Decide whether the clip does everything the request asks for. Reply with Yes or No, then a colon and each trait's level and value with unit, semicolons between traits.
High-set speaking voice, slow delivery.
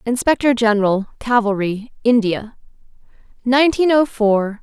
Yes: high, 230 Hz; slow, 90 wpm